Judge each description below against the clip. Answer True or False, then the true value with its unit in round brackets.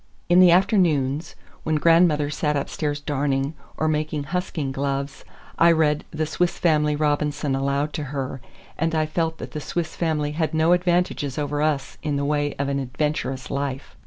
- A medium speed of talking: True (170 wpm)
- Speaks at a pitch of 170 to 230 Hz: False (150 Hz)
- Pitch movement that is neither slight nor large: False (2.3 semitones)